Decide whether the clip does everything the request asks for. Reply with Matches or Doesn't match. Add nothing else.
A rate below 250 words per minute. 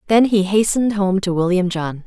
Matches